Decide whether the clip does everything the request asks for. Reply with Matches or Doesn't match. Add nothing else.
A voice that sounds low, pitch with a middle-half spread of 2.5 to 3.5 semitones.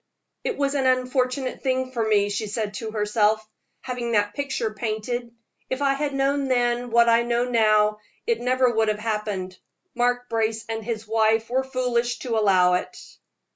Doesn't match